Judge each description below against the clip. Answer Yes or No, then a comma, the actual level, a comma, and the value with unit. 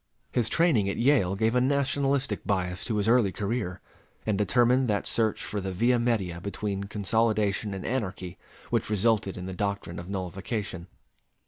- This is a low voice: Yes, low, 105 Hz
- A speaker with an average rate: Yes, average, 160 wpm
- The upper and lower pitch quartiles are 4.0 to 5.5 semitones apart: No, average, 3.5 semitones